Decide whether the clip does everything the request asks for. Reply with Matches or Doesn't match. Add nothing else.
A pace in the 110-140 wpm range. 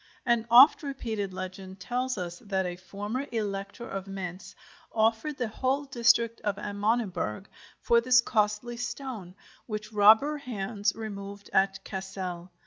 Matches